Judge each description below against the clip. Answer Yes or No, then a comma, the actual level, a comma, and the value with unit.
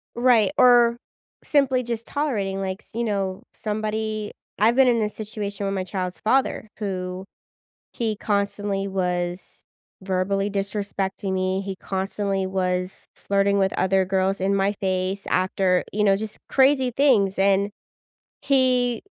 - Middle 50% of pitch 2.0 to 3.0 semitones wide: Yes, narrow, 2.5 semitones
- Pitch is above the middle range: Yes, high, 200 Hz